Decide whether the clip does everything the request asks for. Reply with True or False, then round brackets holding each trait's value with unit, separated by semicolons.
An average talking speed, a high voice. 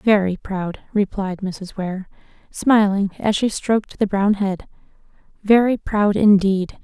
False (125 wpm; 200 Hz)